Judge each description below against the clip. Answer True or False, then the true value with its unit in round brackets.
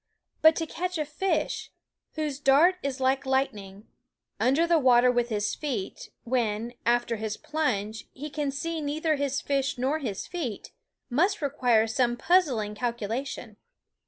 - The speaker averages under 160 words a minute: True (150 wpm)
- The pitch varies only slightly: False (4.6 semitones)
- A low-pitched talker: False (265 Hz)